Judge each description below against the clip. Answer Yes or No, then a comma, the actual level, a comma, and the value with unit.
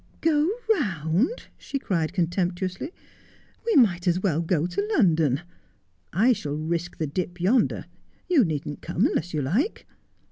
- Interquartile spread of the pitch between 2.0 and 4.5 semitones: No, wide, 5.6 semitones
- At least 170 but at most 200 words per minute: No, average, 155 wpm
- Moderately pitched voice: Yes, medium, 175 Hz